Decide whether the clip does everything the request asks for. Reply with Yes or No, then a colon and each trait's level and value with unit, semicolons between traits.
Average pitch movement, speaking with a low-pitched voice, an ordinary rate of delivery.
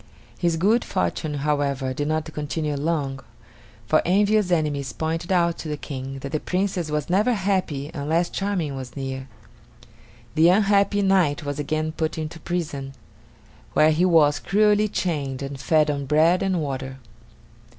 No: average, 4.1 semitones; medium, 155 Hz; average, 150 wpm